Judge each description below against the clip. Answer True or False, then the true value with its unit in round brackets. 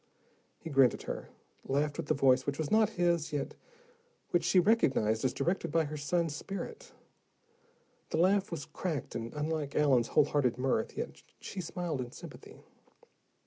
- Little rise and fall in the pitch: False (4.4 semitones)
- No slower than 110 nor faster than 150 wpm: False (165 wpm)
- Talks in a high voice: False (150 Hz)